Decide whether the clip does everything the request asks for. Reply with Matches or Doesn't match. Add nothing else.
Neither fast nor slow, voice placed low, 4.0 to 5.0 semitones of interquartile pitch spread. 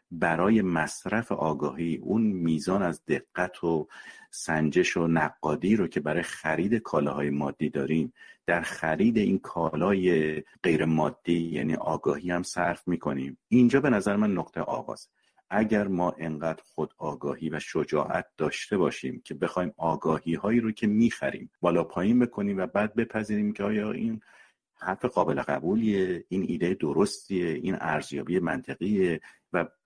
Matches